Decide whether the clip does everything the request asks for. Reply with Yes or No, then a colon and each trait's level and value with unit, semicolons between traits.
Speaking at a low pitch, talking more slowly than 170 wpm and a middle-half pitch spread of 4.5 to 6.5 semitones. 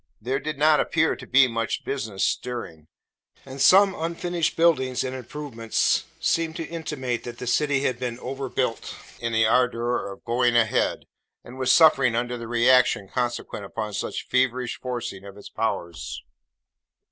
No: low, 125 Hz; average, 160 wpm; average, 2.9 semitones